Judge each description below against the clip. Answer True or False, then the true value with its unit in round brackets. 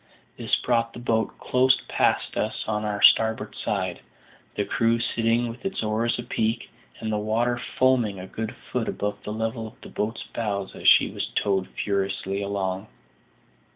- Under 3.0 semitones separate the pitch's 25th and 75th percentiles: True (2.4 semitones)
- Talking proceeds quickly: False (165 wpm)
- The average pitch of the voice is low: True (110 Hz)